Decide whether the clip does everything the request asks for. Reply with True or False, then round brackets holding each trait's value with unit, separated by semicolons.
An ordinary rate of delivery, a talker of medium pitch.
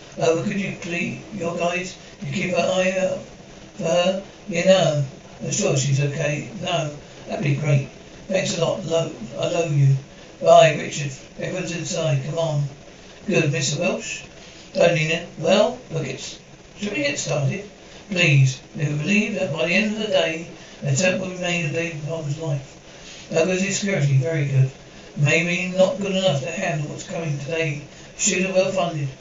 True (180 wpm; 170 Hz)